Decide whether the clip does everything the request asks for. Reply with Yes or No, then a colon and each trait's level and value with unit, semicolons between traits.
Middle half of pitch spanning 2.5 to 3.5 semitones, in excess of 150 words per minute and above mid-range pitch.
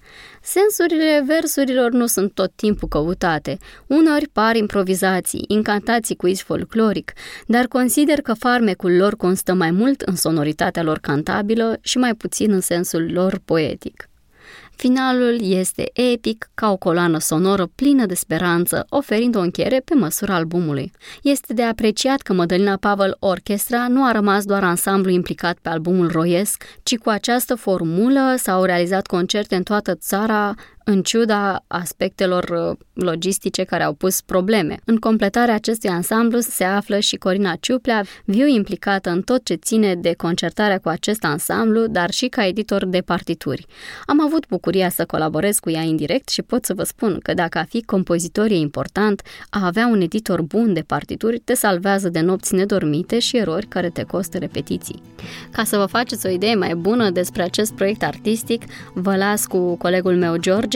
No: average, 4.3 semitones; average, 165 wpm; high, 195 Hz